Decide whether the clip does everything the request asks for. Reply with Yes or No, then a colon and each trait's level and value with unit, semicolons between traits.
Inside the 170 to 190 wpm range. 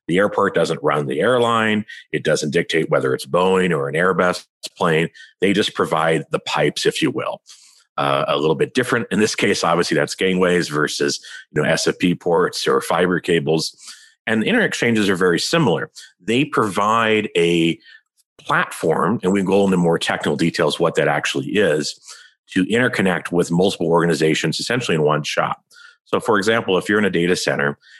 Yes: average, 180 wpm